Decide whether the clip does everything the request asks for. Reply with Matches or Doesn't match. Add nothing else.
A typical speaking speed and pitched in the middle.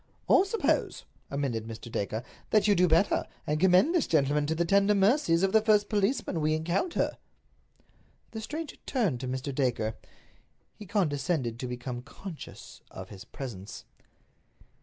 Matches